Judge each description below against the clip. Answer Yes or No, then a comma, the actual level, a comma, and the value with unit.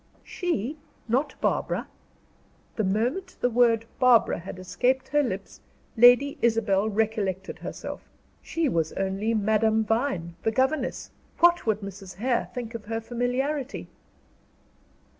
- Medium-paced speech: No, slow, 120 wpm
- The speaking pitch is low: No, high, 230 Hz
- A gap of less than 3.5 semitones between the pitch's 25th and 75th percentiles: No, average, 3.9 semitones